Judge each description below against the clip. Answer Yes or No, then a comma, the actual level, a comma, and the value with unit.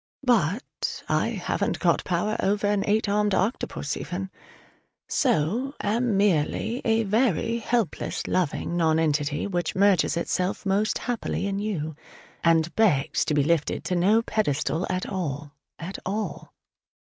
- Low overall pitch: No, high, 195 Hz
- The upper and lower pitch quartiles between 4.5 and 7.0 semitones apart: Yes, average, 4.8 semitones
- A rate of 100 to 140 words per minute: Yes, slow, 135 wpm